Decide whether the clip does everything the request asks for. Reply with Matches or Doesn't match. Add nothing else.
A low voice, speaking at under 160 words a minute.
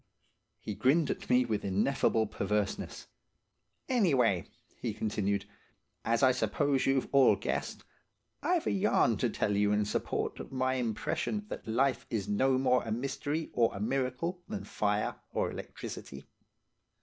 Matches